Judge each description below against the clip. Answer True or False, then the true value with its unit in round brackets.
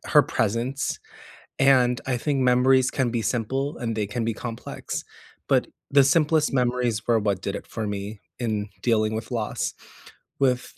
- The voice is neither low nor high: False (120 Hz)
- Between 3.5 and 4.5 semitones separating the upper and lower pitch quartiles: False (3.1 semitones)